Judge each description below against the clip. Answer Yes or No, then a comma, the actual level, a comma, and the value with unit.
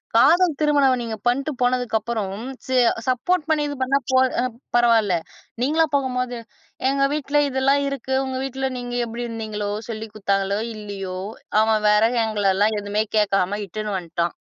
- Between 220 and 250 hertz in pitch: Yes, high, 235 Hz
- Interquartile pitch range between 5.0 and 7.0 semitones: No, average, 4.2 semitones